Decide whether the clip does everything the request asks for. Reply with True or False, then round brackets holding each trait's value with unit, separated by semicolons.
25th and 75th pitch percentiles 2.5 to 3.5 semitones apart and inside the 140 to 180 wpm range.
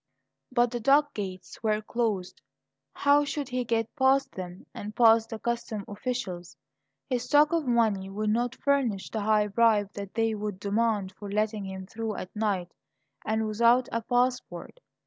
True (3.1 semitones; 165 wpm)